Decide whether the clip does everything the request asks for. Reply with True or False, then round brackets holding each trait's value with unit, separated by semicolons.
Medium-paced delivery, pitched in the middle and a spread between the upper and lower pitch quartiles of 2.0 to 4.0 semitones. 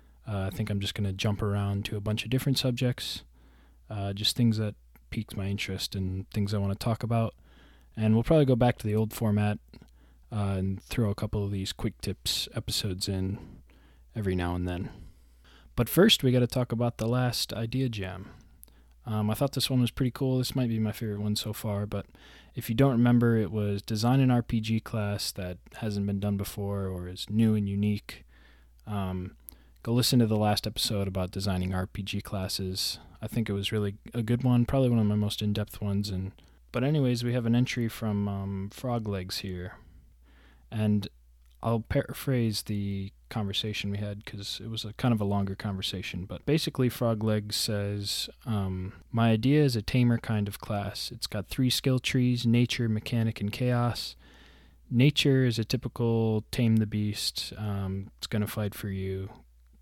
False (190 wpm; 105 Hz; 3.4 semitones)